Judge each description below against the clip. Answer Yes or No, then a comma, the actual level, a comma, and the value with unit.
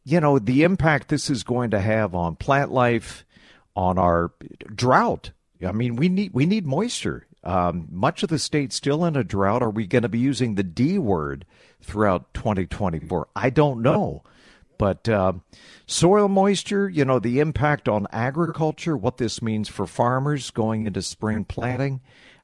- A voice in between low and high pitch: No, low, 120 Hz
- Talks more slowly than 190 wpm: Yes, average, 170 wpm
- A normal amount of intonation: No, wide, 6.6 semitones